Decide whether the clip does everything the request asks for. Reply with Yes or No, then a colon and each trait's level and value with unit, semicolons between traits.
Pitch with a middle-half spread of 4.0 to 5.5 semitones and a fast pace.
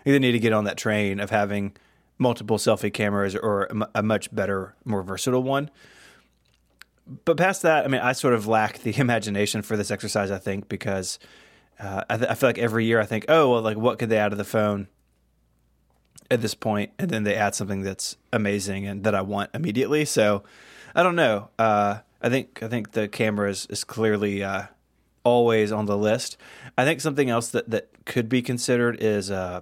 No: average, 3.1 semitones; fast, 215 wpm